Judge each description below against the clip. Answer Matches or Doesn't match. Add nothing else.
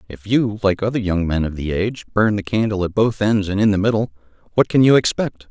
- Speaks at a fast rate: Matches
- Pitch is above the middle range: Doesn't match